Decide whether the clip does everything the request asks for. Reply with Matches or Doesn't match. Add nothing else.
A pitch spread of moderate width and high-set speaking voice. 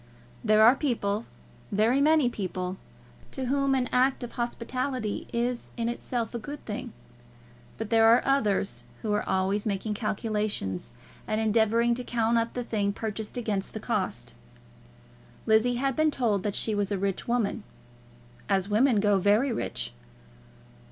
Matches